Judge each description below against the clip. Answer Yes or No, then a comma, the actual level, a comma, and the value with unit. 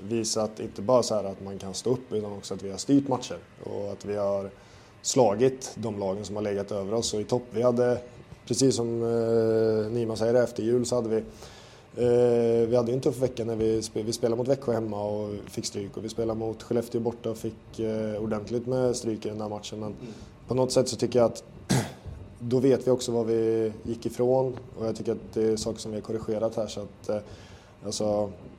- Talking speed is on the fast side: Yes, fast, 215 wpm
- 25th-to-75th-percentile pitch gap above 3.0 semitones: No, narrow, 2.4 semitones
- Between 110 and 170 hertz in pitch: Yes, low, 115 Hz